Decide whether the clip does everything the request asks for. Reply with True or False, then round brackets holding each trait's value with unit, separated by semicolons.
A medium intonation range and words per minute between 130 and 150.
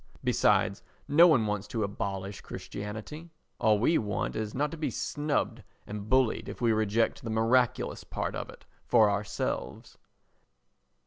True (4.0 semitones; 140 wpm)